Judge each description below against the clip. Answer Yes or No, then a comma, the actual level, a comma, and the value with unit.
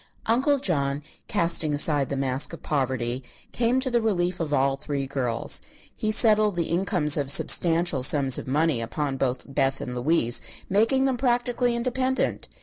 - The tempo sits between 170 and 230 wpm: No, average, 160 wpm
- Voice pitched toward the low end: No, medium, 155 Hz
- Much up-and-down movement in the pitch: Yes, wide, 8.6 semitones